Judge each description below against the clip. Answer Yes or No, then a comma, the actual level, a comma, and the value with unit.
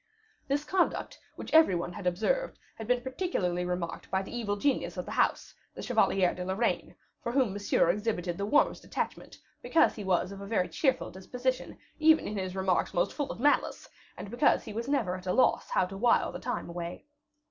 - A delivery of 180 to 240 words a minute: Yes, average, 200 wpm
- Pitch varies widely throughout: Yes, wide, 5.9 semitones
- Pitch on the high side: Yes, high, 205 Hz